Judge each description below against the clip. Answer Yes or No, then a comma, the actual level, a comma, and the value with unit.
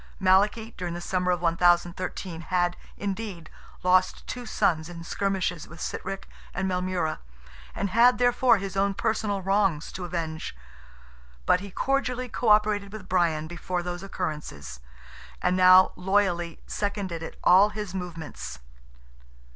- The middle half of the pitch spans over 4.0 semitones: No, narrow, 2.6 semitones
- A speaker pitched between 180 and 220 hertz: Yes, medium, 185 Hz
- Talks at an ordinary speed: No, slow, 130 wpm